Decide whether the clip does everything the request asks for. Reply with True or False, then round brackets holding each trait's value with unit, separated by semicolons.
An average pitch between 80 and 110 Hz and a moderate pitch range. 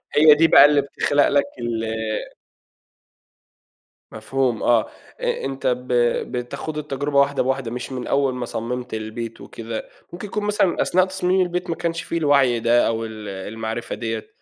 False (130 Hz; 4.7 semitones)